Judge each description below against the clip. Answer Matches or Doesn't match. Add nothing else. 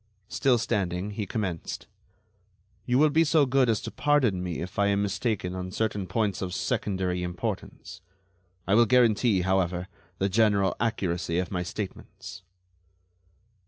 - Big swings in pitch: Doesn't match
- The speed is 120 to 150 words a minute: Matches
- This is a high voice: Doesn't match